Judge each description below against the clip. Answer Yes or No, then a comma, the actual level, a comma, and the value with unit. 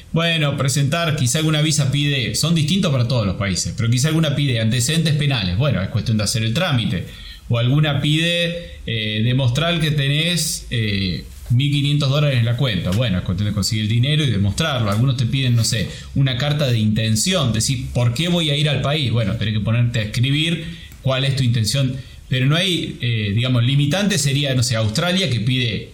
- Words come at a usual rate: No, fast, 200 wpm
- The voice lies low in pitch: Yes, low, 130 Hz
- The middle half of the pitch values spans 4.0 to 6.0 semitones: Yes, average, 4.6 semitones